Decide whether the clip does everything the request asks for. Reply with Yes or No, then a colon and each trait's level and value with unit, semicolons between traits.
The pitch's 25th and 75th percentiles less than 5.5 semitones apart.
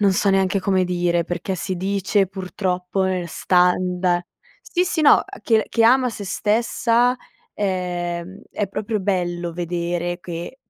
Yes: narrow, 2.5 semitones